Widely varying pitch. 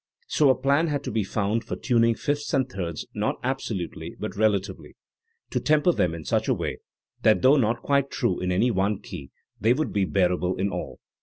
Yes: wide, 6.2 semitones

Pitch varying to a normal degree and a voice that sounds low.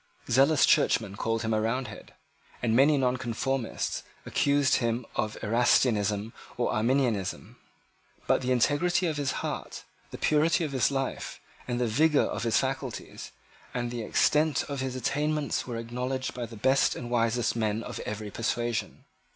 Yes: average, 3.2 semitones; low, 125 Hz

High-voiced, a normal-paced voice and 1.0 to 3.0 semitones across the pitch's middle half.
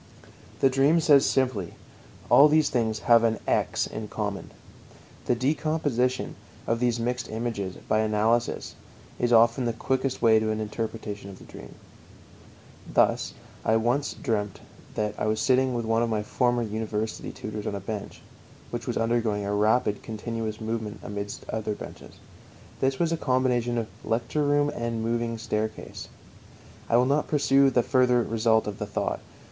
No: low, 115 Hz; average, 160 wpm; average, 2.7 semitones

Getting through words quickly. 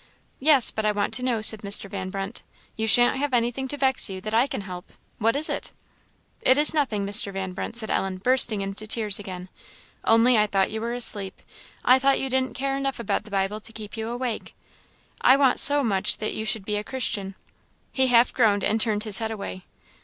Yes: fast, 220 wpm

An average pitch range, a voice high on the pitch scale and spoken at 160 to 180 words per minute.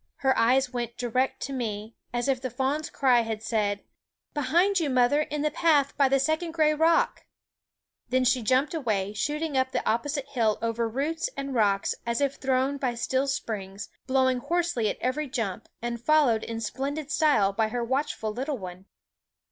No: average, 3.9 semitones; very high, 260 Hz; average, 190 wpm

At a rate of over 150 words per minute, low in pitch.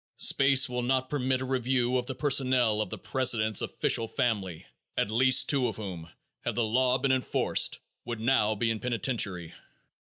Yes: average, 170 wpm; low, 125 Hz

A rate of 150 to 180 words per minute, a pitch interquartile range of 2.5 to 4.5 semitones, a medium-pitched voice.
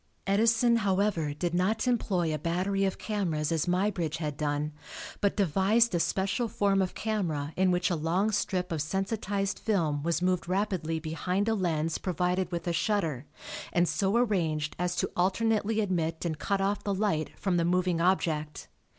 Yes: average, 170 wpm; average, 3.5 semitones; medium, 180 Hz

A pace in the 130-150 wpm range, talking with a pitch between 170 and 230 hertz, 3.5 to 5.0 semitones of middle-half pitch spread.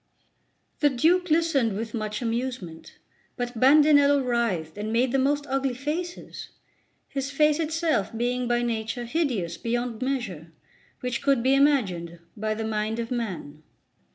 No: average, 140 wpm; high, 245 Hz; average, 4.2 semitones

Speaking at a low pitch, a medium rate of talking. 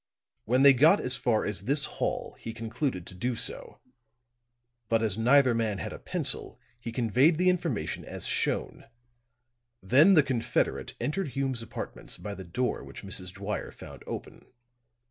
Yes: low, 120 Hz; average, 160 wpm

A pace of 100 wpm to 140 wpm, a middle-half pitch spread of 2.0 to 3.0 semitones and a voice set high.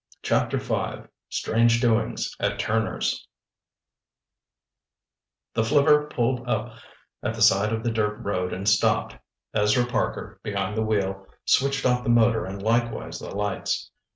No: slow, 135 wpm; narrow, 2.6 semitones; low, 110 Hz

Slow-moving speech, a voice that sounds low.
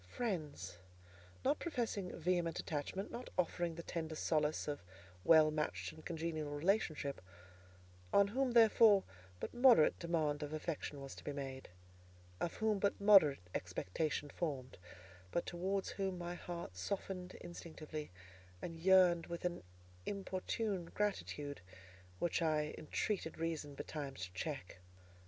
No: slow, 130 wpm; medium, 165 Hz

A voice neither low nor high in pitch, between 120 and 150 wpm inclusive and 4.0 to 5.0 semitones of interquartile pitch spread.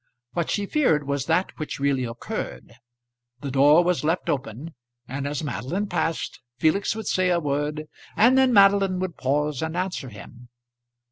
No: medium, 155 Hz; average, 160 wpm; average, 4.7 semitones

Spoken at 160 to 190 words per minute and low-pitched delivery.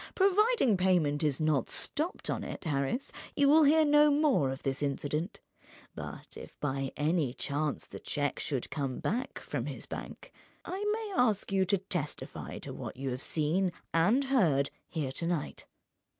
No: average, 165 wpm; medium, 170 Hz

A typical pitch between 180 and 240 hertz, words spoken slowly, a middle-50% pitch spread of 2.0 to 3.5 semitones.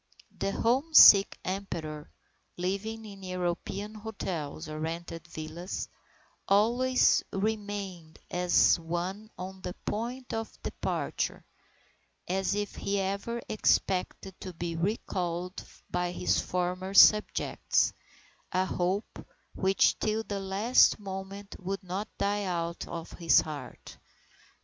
Yes: high, 190 Hz; slow, 110 wpm; average, 2.8 semitones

